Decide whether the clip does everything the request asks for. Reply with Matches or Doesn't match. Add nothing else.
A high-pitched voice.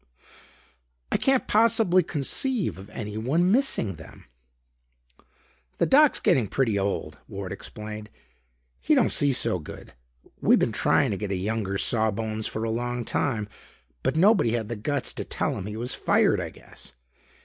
Doesn't match